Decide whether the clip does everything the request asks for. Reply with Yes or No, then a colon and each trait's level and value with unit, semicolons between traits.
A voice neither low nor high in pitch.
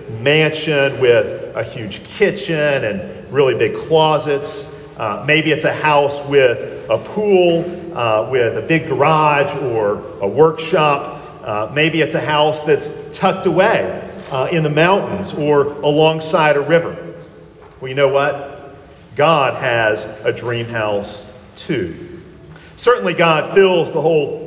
Yes: medium, 150 Hz